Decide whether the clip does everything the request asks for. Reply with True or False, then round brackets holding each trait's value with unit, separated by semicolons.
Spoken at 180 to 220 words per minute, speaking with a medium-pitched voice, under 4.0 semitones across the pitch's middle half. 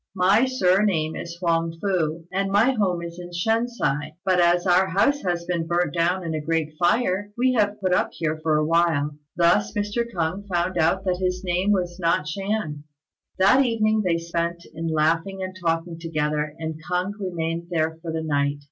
True (190 wpm; 175 Hz; 2.9 semitones)